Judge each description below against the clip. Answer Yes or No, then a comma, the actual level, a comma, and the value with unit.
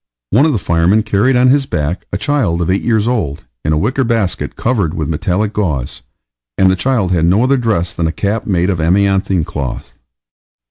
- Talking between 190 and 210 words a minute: Yes, average, 195 wpm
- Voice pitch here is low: Yes, very low, 95 Hz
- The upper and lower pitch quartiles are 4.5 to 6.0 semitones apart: Yes, wide, 5.4 semitones